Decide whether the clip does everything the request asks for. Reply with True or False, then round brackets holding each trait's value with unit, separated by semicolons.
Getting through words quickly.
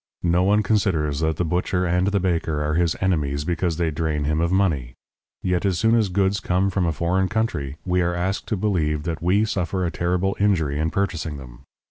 True (210 wpm)